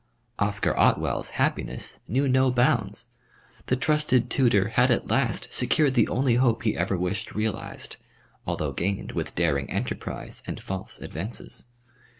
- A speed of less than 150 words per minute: Yes, average, 140 wpm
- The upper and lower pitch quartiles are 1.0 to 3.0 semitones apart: No, average, 4.7 semitones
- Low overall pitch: Yes, low, 115 Hz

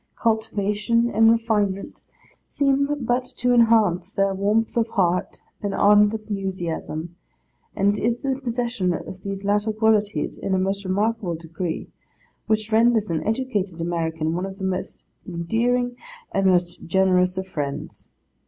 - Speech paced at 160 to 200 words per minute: No, average, 140 wpm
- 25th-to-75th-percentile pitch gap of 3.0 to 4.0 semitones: Yes, average, 3.5 semitones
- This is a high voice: Yes, high, 205 Hz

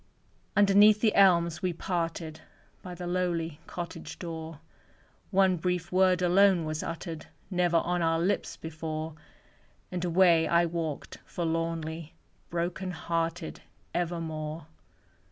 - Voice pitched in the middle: Yes, medium, 170 Hz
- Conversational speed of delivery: No, slow, 115 wpm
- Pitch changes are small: Yes, narrow, 1.8 semitones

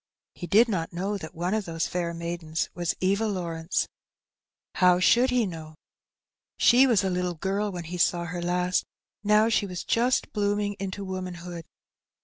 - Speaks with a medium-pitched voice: Yes, medium, 180 Hz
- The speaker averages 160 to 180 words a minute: Yes, average, 170 wpm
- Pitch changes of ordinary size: Yes, average, 3.1 semitones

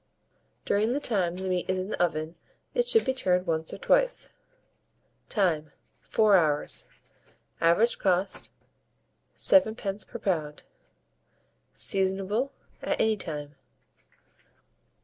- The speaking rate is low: Yes, slow, 110 wpm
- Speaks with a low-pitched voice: No, high, 190 Hz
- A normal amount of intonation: Yes, average, 4.4 semitones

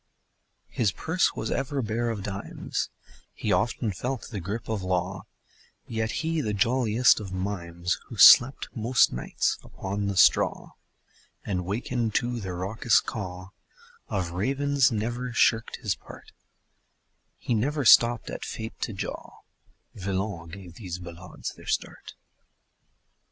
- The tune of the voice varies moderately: Yes, average, 4.3 semitones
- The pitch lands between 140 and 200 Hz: No, low, 105 Hz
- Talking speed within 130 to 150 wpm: Yes, slow, 135 wpm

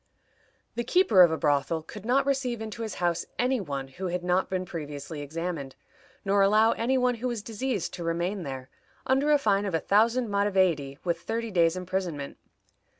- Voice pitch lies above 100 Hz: Yes, high, 190 Hz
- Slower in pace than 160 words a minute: No, average, 185 wpm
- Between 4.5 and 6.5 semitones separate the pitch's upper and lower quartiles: Yes, wide, 5.6 semitones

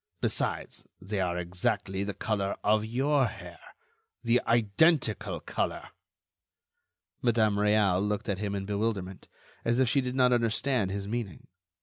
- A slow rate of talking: Yes, slow, 130 wpm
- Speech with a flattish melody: No, average, 3.2 semitones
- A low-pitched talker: Yes, low, 105 Hz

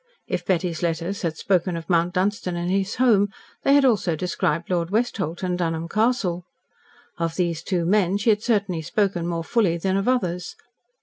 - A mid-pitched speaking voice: Yes, medium, 180 Hz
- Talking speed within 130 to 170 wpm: No, average, 180 wpm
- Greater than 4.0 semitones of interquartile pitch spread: No, average, 3.2 semitones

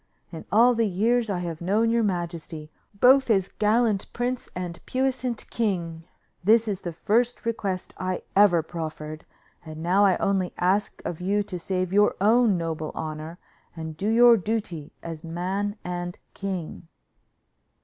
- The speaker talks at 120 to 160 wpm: Yes, average, 150 wpm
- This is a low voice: No, high, 190 Hz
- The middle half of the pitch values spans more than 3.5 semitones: Yes, average, 4.5 semitones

